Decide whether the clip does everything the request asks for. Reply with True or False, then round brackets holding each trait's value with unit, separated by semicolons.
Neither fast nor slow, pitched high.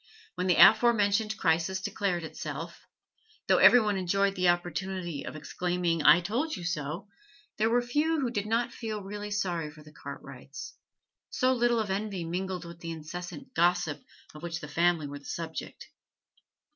False (170 wpm; 180 Hz)